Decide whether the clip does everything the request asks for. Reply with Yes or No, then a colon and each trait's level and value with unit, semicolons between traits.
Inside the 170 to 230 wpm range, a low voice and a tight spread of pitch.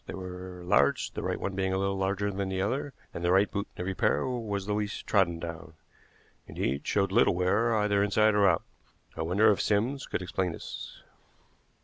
Yes: fast, 205 wpm; very low, 95 Hz; narrow, 2.2 semitones